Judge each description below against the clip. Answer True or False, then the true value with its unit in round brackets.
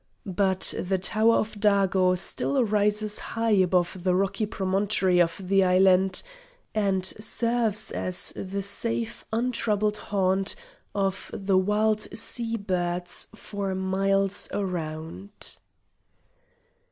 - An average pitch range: False (2.3 semitones)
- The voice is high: True (195 Hz)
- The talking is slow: True (105 wpm)